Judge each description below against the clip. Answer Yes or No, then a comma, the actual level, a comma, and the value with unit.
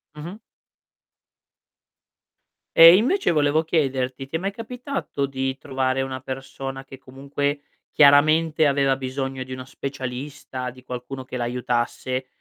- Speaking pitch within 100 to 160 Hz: Yes, low, 135 Hz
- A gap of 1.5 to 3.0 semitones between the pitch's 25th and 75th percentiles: Yes, narrow, 2.6 semitones